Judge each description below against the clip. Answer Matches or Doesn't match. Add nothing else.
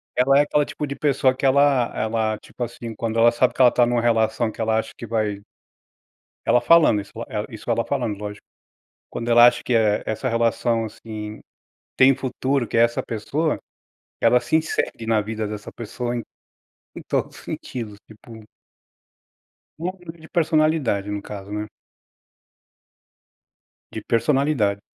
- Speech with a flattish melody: Doesn't match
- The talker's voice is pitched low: Matches